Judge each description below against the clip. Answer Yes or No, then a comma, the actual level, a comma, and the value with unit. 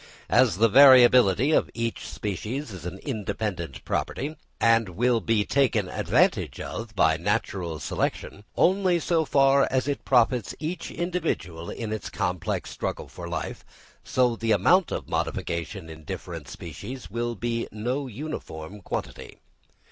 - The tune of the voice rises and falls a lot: Yes, wide, 6.1 semitones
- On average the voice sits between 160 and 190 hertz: No, low, 115 Hz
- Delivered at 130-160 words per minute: Yes, average, 140 wpm